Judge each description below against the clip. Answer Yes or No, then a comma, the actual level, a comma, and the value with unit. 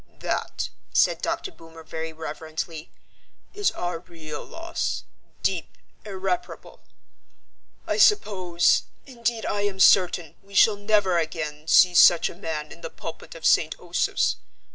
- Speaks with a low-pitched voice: No, medium, 175 Hz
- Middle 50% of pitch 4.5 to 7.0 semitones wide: No, average, 3.9 semitones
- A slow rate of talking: Yes, slow, 130 wpm